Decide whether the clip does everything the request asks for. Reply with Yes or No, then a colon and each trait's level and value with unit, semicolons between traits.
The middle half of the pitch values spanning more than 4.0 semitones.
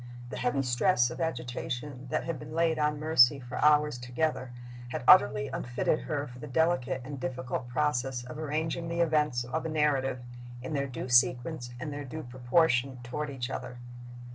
No: average, 3.7 semitones